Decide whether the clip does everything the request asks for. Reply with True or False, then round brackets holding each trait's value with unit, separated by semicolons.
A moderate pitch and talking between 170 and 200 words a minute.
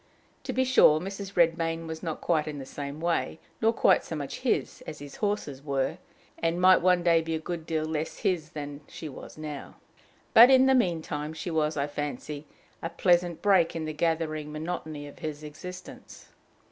True (160 Hz; 195 wpm)